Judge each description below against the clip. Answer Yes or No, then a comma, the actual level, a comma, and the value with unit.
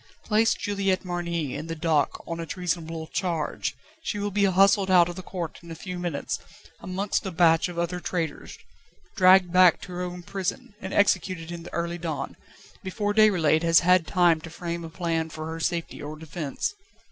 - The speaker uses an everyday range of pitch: No, narrow, 2.2 semitones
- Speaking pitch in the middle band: Yes, medium, 175 Hz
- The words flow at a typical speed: Yes, average, 190 wpm